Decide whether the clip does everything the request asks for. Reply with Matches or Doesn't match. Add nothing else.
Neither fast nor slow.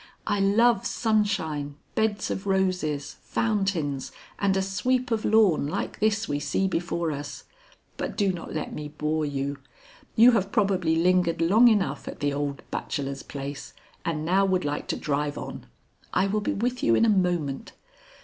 Matches